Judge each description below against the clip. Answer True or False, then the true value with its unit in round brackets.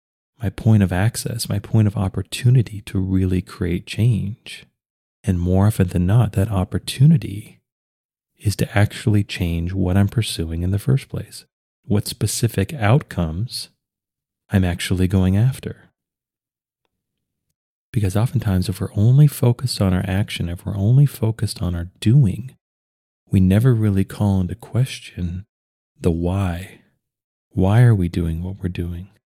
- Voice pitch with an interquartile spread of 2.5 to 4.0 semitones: True (3.7 semitones)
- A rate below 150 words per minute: True (140 wpm)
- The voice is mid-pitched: False (100 Hz)